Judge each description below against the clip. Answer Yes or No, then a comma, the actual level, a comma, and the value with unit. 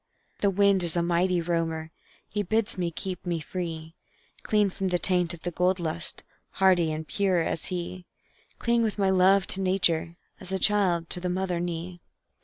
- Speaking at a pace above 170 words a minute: Yes, average, 185 wpm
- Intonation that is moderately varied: No, narrow, 2.1 semitones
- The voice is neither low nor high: Yes, medium, 180 Hz